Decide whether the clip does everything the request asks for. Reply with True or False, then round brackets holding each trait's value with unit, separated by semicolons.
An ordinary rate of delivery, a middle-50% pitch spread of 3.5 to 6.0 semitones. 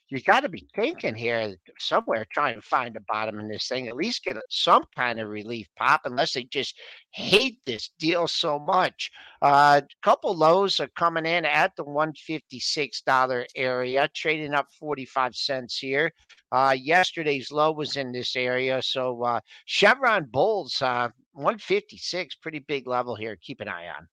True (170 wpm; 4.2 semitones)